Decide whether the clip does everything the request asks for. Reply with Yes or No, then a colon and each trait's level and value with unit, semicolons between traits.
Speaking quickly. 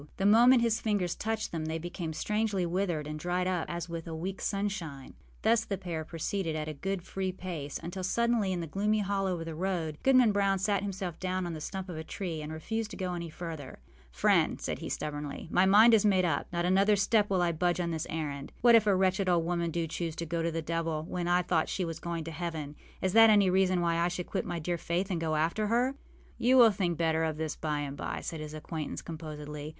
Yes: fast, 240 wpm